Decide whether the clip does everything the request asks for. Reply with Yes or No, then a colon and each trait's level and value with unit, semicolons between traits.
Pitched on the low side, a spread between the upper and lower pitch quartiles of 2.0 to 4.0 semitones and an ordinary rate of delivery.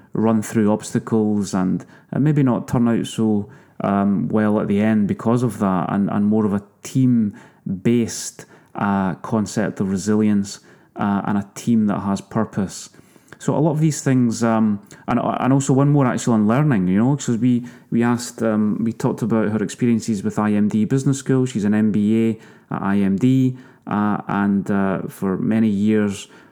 Yes: low, 110 Hz; average, 3.1 semitones; average, 175 wpm